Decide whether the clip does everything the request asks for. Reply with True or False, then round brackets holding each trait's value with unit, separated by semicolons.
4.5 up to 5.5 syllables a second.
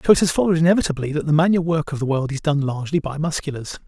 False (7.6 syllables/s)